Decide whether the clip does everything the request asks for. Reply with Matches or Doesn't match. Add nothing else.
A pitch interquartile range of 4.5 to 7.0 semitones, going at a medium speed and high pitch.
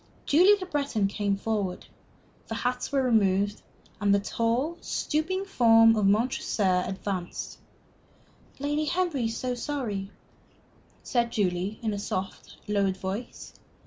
Doesn't match